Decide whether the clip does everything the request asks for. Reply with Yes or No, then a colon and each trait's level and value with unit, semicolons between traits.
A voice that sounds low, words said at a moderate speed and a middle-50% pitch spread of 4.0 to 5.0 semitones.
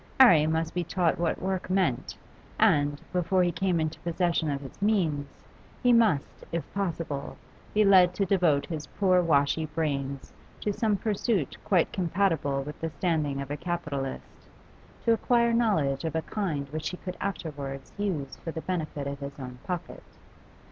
No: medium, 165 Hz; average, 165 wpm; average, 4.7 semitones